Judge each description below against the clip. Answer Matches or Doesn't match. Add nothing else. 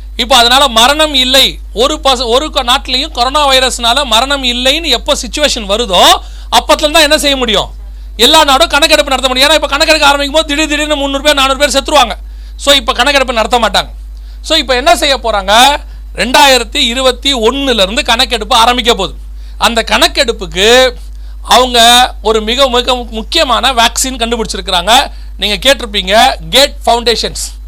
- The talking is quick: Matches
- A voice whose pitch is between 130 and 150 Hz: Doesn't match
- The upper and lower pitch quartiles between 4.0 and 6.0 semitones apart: Doesn't match